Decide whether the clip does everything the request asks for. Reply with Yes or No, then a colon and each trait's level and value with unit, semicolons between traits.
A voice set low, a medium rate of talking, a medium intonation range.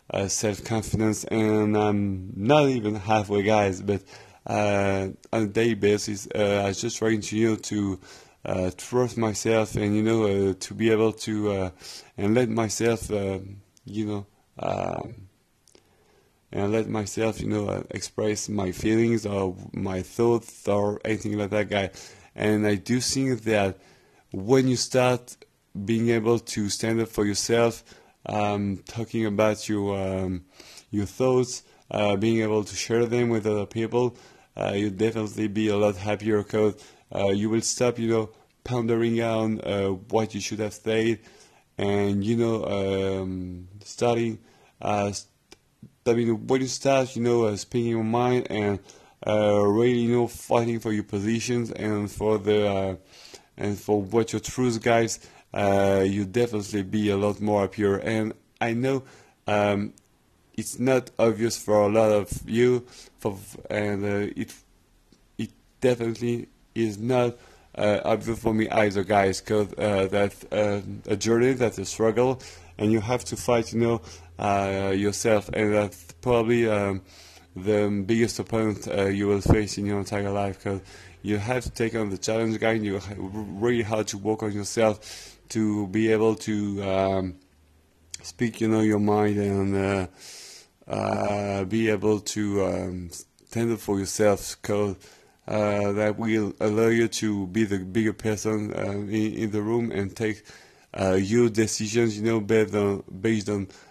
No: low, 105 Hz; average, 165 wpm; narrow, 2.1 semitones